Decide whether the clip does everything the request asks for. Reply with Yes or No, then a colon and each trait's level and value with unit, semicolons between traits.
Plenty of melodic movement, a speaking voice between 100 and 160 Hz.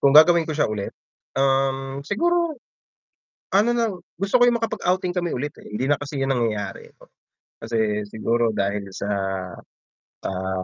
Yes: wide, 8.7 semitones; low, 135 Hz